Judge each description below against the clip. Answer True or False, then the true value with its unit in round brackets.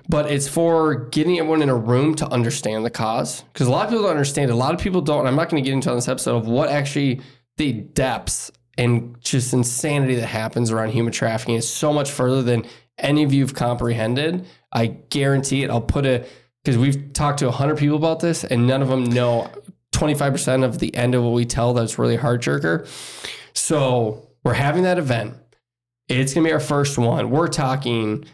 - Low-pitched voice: True (130 Hz)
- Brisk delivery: True (220 wpm)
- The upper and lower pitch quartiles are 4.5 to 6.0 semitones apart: False (3.6 semitones)